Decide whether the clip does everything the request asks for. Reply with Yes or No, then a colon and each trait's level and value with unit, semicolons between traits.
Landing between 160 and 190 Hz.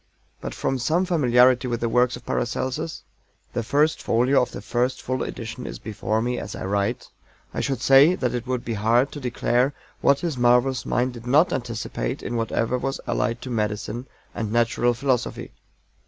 No: low, 125 Hz